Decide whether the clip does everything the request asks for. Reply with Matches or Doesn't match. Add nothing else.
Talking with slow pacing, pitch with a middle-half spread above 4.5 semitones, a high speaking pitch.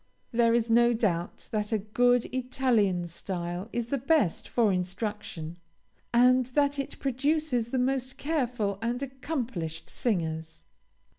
Matches